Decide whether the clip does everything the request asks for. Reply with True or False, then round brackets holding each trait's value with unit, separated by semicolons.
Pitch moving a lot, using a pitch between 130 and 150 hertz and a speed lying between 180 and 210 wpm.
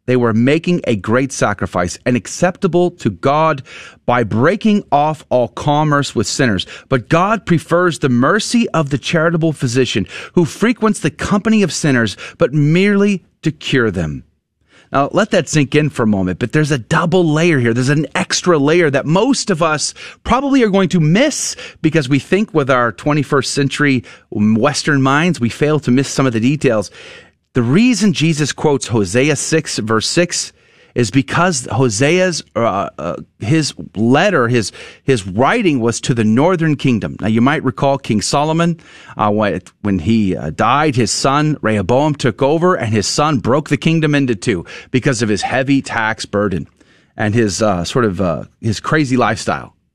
False (5.7 semitones; 140 Hz; 170 wpm)